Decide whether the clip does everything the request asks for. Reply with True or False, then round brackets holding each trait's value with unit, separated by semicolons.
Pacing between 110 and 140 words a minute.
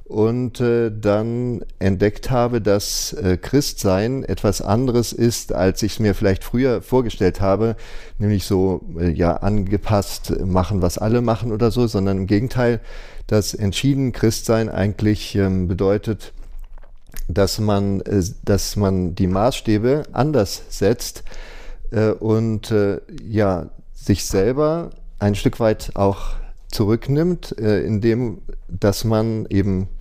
True (130 wpm)